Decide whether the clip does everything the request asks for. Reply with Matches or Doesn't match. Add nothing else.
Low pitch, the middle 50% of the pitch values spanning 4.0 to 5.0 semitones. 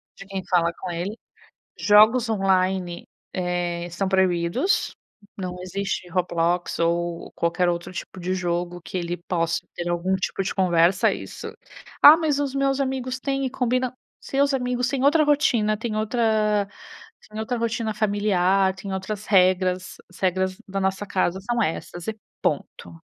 Doesn't match